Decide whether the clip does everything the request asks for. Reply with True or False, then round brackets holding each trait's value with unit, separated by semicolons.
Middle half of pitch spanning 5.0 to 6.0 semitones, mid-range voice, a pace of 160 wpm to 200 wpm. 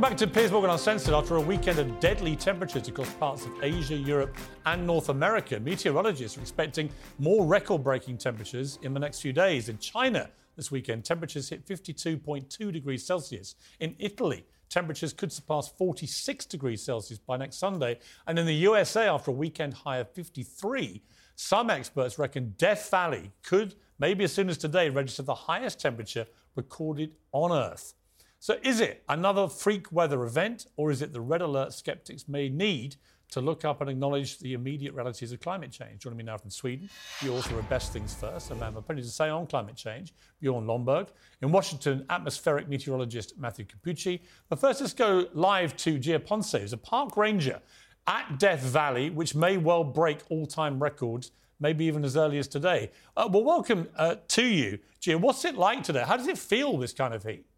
True (5.5 semitones; 150 Hz; 190 wpm)